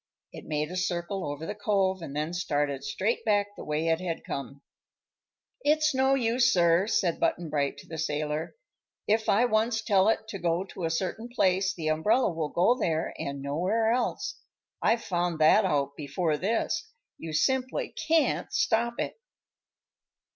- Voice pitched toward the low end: No, medium, 180 Hz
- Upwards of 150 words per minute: Yes, average, 170 wpm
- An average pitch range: No, wide, 6.0 semitones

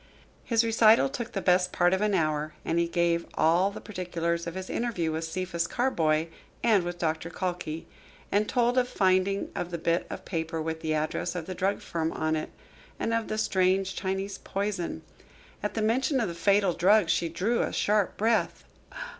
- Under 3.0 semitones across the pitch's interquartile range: No, average, 3.7 semitones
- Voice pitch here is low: No, medium, 185 Hz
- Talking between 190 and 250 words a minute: Yes, average, 195 wpm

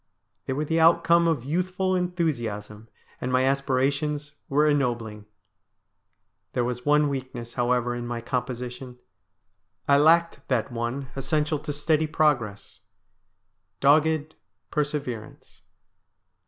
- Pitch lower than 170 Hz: Yes, low, 135 Hz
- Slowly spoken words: Yes, slow, 115 wpm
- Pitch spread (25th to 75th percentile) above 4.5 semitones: No, average, 4.0 semitones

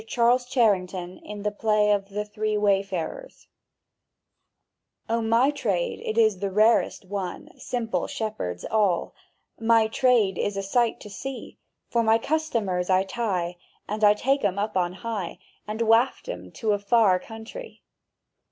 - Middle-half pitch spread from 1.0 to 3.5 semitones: Yes, average, 2.9 semitones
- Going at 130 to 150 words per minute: Yes, average, 145 wpm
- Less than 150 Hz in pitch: No, high, 215 Hz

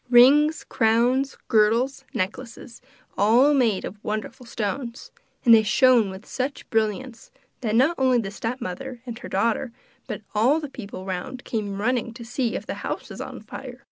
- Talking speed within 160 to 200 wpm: Yes, average, 165 wpm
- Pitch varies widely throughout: No, average, 3.3 semitones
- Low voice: No, high, 235 Hz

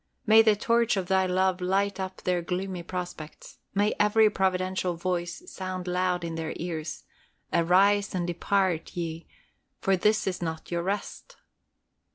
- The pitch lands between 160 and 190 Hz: Yes, medium, 185 Hz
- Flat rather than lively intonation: Yes, narrow, 2.0 semitones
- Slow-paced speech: No, average, 150 wpm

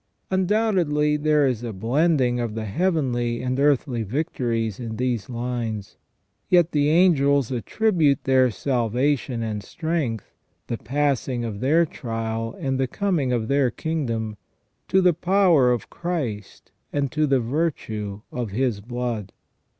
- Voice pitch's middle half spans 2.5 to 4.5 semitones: No, average, 4.9 semitones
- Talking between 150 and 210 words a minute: No, average, 140 wpm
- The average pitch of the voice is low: Yes, low, 130 Hz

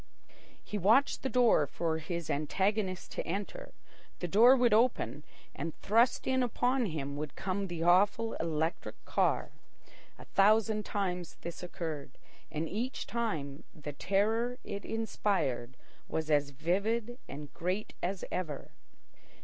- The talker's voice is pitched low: No, medium, 185 Hz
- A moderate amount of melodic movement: No, wide, 6.0 semitones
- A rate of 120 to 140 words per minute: Yes, slow, 135 wpm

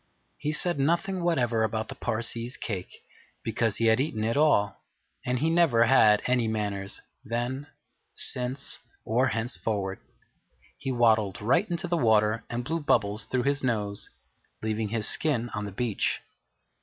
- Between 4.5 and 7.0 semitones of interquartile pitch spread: No, average, 3.9 semitones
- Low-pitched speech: Yes, low, 115 Hz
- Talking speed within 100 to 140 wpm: No, average, 150 wpm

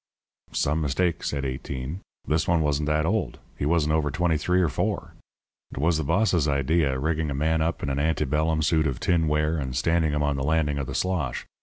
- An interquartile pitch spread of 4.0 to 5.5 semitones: No, narrow, 2.4 semitones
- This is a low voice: Yes, very low, 75 Hz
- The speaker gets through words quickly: Yes, fast, 210 wpm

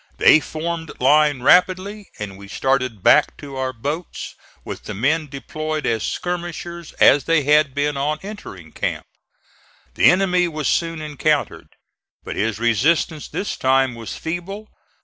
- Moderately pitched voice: Yes, medium, 150 Hz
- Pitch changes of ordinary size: Yes, average, 4.5 semitones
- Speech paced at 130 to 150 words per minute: Yes, average, 145 wpm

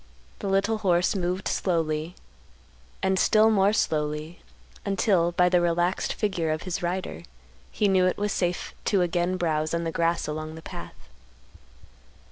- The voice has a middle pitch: Yes, medium, 175 Hz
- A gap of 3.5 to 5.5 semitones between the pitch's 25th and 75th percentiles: No, average, 2.7 semitones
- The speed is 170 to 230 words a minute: No, average, 150 wpm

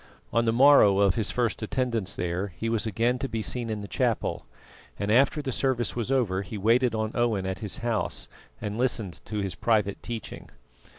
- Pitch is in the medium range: No, low, 115 Hz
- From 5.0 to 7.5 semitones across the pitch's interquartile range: No, average, 3.0 semitones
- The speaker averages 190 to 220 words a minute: Yes, average, 195 wpm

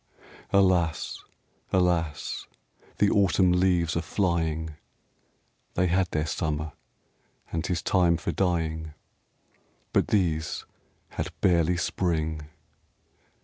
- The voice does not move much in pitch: Yes, narrow, 2.3 semitones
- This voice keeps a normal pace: No, slow, 95 wpm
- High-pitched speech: No, very low, 85 Hz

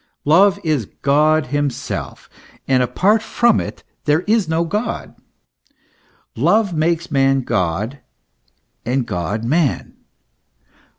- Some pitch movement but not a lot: Yes, average, 5.0 semitones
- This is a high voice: No, medium, 150 Hz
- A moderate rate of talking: No, slow, 105 wpm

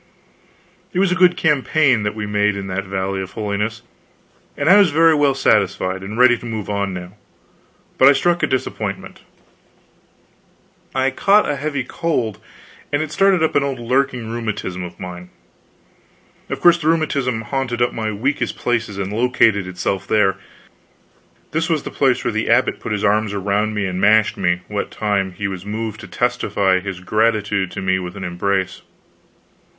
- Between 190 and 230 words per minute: No, average, 175 wpm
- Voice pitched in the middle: No, low, 110 Hz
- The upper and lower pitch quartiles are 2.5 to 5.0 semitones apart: No, wide, 5.6 semitones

